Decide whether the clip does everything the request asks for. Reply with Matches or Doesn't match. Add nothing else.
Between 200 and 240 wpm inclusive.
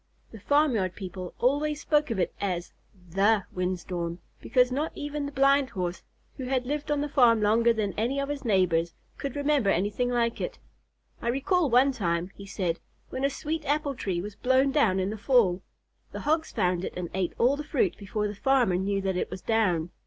Matches